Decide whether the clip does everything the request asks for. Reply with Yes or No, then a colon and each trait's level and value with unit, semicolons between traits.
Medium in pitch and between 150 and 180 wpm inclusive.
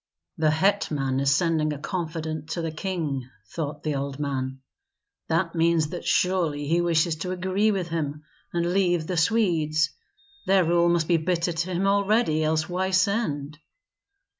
Yes: medium, 165 Hz; average, 160 wpm